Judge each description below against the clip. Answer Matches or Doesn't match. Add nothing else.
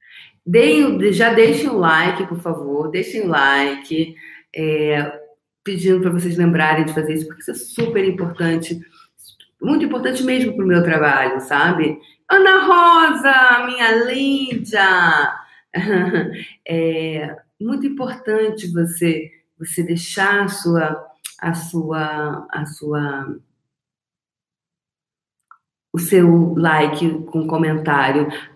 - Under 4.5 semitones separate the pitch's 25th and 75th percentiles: Doesn't match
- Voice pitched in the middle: Matches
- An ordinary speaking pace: Doesn't match